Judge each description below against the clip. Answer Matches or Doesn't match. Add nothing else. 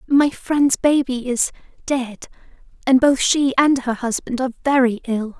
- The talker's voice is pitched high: Matches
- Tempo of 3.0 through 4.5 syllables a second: Matches